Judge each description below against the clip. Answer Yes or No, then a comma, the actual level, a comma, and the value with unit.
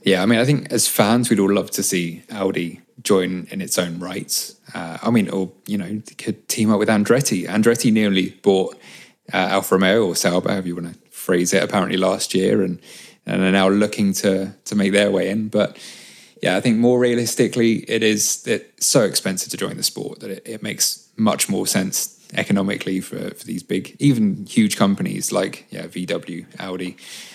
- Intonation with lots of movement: No, average, 3.2 semitones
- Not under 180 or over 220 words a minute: Yes, average, 200 wpm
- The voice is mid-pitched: No, low, 100 Hz